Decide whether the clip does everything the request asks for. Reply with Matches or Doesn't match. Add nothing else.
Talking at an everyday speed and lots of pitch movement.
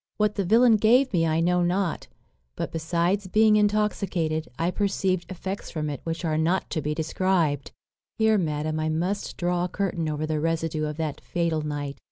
Doesn't match